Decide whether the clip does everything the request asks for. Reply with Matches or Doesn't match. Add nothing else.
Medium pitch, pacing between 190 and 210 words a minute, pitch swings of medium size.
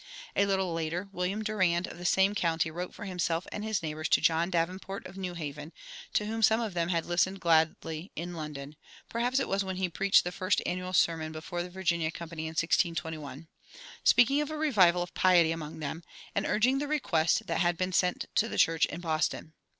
Matches